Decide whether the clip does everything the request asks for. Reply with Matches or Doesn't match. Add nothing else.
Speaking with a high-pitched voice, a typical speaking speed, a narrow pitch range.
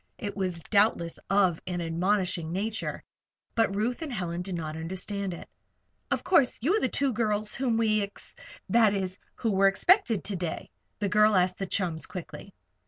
Doesn't match